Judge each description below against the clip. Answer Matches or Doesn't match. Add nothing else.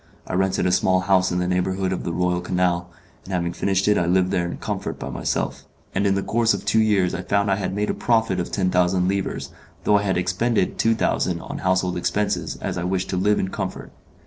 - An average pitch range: Doesn't match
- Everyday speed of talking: Doesn't match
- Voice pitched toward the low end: Matches